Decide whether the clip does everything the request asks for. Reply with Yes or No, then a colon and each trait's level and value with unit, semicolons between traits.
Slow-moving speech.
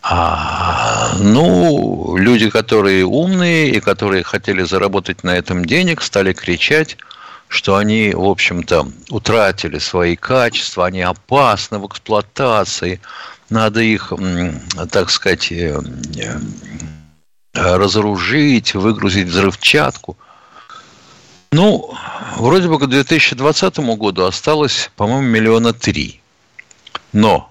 Yes: slow, 95 wpm